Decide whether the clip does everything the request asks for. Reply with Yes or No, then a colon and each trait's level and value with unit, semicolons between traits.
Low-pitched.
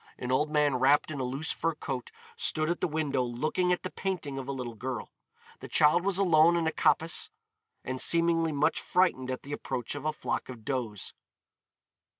No: medium, 150 Hz